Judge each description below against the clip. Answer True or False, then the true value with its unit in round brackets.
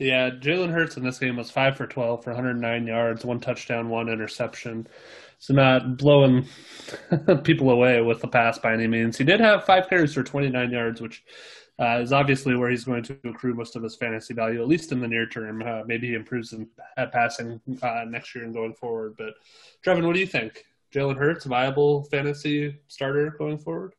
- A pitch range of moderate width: True (3.5 semitones)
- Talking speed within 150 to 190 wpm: False (205 wpm)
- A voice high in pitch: False (125 Hz)